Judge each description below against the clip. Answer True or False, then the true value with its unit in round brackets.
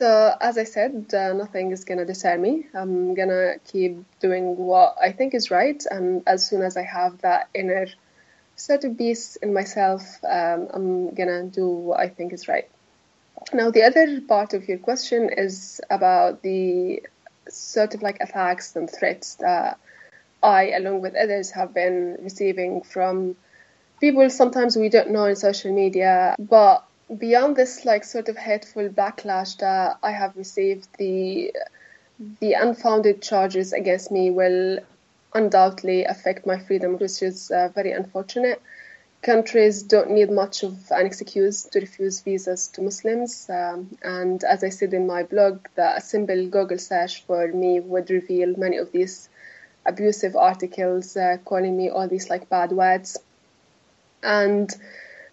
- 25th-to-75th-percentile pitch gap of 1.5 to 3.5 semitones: True (3.0 semitones)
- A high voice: True (195 Hz)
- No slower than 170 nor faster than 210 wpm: False (155 wpm)